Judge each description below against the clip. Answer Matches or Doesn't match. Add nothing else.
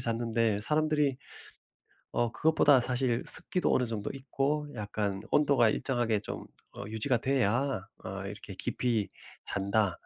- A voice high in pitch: Doesn't match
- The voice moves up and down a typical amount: Matches